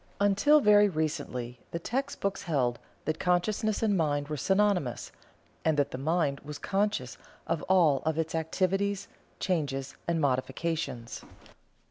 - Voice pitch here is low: No, medium, 165 Hz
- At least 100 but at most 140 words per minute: Yes, slow, 135 wpm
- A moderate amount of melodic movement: No, wide, 5.7 semitones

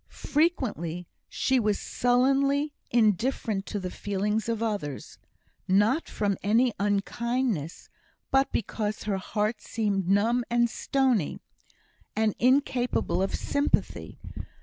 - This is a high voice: Yes, high, 220 Hz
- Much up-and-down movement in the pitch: No, average, 3.8 semitones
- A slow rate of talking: Yes, slow, 105 wpm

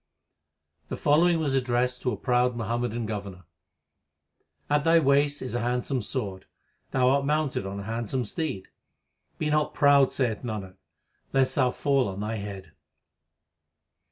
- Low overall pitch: Yes, low, 125 Hz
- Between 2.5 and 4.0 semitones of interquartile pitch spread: No, average, 4.5 semitones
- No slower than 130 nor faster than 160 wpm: Yes, average, 150 wpm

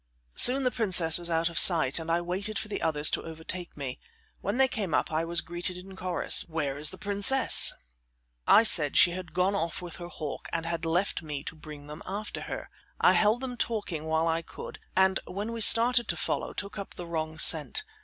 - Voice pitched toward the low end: No, medium, 175 Hz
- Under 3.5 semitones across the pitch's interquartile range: No, average, 3.9 semitones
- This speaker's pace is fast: Yes, fast, 215 wpm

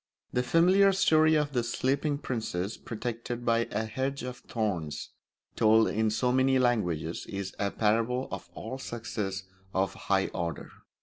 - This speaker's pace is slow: No, average, 150 wpm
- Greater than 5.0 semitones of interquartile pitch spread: No, average, 4.0 semitones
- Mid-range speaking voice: No, low, 115 Hz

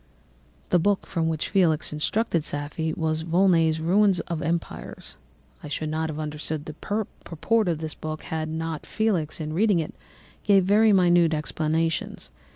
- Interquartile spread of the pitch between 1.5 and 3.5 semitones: Yes, average, 2.9 semitones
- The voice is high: No, medium, 160 Hz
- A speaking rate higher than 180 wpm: No, average, 155 wpm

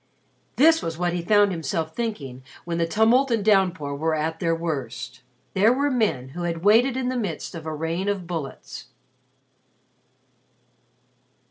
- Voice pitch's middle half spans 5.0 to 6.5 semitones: Yes, average, 5.3 semitones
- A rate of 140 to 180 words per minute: Yes, average, 155 wpm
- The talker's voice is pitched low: No, medium, 175 Hz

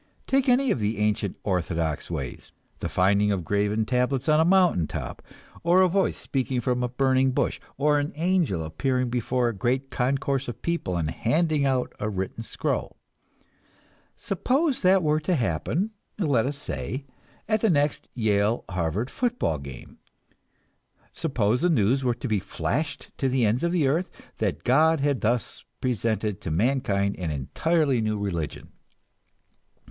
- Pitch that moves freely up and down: Yes, wide, 6.9 semitones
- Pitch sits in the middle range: No, low, 125 Hz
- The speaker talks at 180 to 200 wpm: No, average, 160 wpm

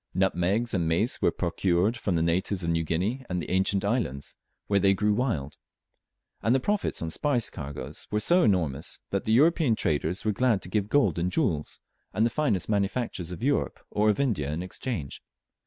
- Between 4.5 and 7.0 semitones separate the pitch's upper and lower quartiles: Yes, wide, 5.4 semitones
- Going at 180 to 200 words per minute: Yes, average, 190 wpm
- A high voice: No, low, 100 Hz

